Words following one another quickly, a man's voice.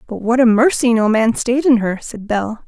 No: fast, 245 wpm; female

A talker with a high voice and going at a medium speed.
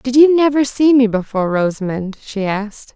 Yes: high, 235 Hz; average, 185 wpm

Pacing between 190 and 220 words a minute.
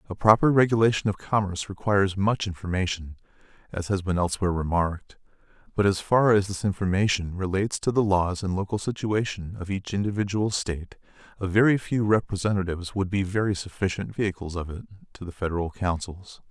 No: average, 165 wpm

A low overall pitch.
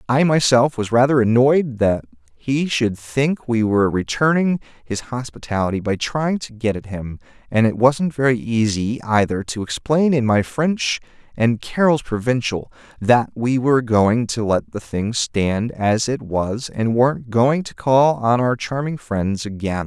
Yes: low, 120 Hz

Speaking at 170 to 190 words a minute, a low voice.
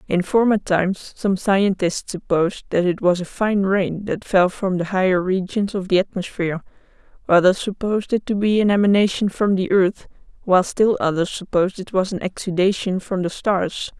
No: average, 180 wpm; high, 190 Hz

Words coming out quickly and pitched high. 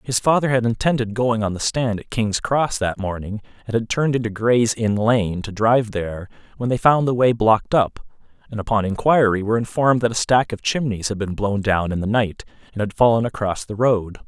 No: fast, 225 wpm; low, 110 Hz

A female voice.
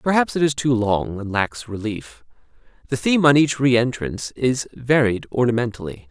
No: male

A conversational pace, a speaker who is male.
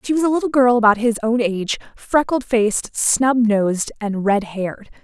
No: average, 190 wpm; female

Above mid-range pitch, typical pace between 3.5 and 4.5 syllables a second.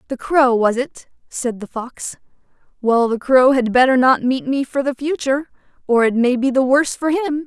No: very high, 260 Hz; 4.9 syllables/s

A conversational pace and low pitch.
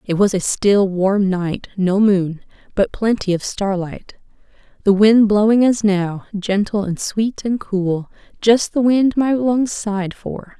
No: average, 165 wpm; high, 205 Hz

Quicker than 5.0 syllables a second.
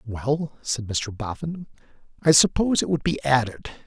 No: 4.8 syllables/s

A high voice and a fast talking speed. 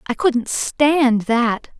No: very high, 255 Hz; slow, 135 wpm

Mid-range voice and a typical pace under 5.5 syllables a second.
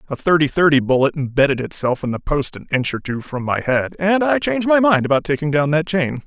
No: medium, 150 Hz; 5.9 syllables/s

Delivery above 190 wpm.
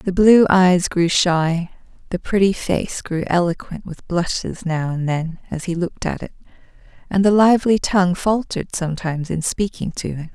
No: average, 175 wpm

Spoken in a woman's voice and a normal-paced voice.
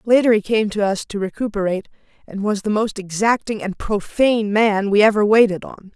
Yes: female; average, 190 wpm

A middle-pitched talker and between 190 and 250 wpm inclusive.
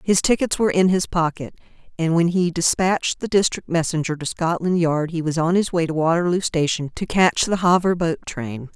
Yes: medium, 170 Hz; fast, 205 wpm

